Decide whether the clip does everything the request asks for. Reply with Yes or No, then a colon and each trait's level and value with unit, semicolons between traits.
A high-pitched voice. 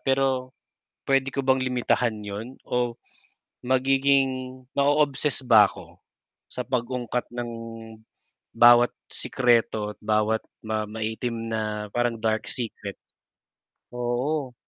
No: low, 120 Hz